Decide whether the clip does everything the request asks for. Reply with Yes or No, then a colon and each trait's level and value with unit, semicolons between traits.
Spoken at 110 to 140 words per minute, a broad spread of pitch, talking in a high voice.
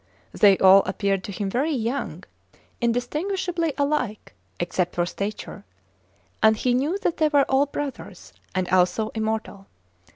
Yes: slow, 135 wpm; wide, 6.6 semitones; high, 230 Hz